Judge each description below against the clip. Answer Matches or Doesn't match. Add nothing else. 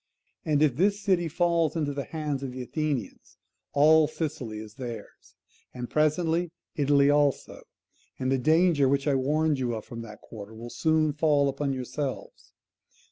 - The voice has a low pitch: Doesn't match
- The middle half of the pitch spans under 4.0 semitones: Matches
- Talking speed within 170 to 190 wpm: Doesn't match